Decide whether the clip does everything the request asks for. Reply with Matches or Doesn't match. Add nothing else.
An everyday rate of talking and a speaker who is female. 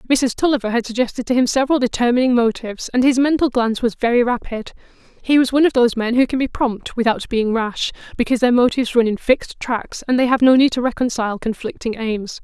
Doesn't match